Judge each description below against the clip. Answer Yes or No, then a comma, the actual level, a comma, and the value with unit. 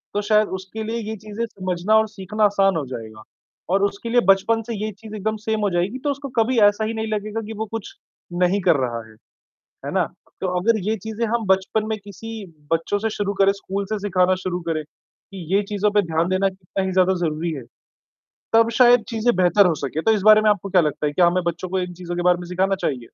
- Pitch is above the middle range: Yes, high, 200 Hz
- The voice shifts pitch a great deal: No, average, 3.4 semitones